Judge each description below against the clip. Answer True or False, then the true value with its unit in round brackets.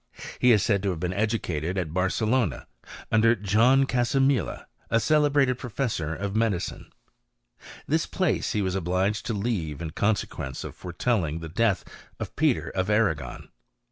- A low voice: True (105 Hz)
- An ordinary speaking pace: True (150 wpm)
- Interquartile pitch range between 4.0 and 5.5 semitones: True (5.0 semitones)